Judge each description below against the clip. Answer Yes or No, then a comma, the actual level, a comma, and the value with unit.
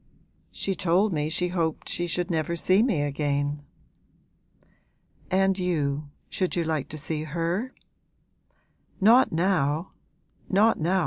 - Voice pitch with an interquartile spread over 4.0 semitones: No, average, 3.7 semitones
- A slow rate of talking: Yes, slow, 125 wpm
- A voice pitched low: No, medium, 170 Hz